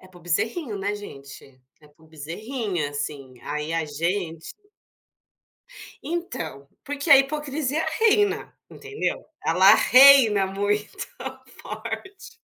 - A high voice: Yes, high, 200 Hz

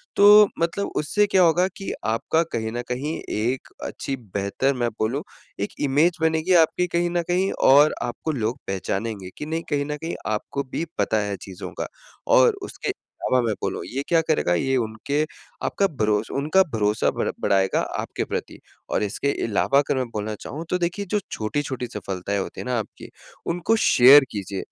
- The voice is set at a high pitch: No, medium, 140 Hz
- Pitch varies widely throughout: Yes, wide, 7.3 semitones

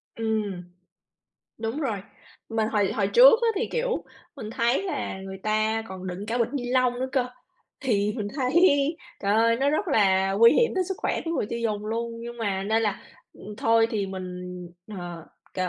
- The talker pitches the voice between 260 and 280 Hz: No, high, 225 Hz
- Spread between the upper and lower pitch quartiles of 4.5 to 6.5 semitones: No, average, 3.7 semitones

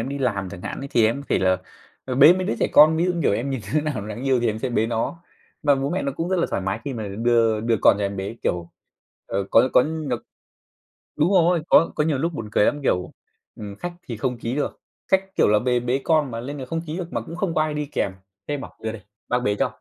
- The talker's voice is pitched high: No, low, 130 Hz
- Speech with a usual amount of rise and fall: No, wide, 5.7 semitones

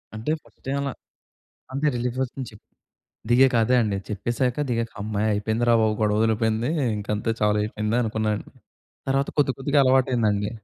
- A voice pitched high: No, low, 115 Hz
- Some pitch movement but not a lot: Yes, average, 3.4 semitones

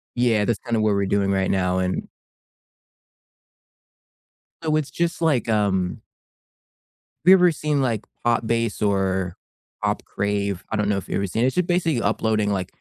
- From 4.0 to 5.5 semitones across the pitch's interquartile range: Yes, average, 4.9 semitones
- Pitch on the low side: Yes, low, 110 Hz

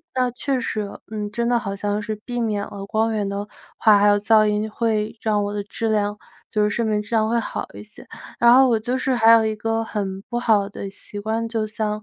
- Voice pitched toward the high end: Yes, high, 215 Hz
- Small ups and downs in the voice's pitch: Yes, narrow, 1.8 semitones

